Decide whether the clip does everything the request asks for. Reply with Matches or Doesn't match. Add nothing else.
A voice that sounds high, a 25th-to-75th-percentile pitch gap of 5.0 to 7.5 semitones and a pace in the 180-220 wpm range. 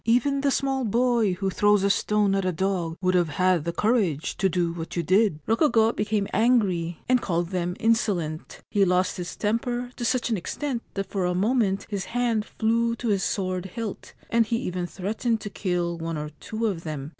Doesn't match